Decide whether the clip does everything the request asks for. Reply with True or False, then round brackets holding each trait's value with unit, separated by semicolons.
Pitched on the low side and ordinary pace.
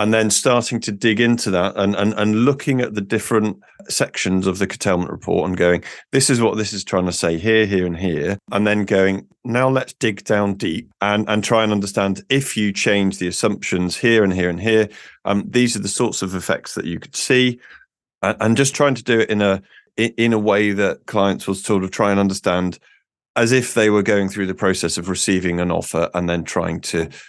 False (105 Hz; 225 wpm)